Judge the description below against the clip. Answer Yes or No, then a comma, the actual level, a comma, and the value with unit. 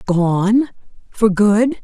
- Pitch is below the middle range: No, high, 210 Hz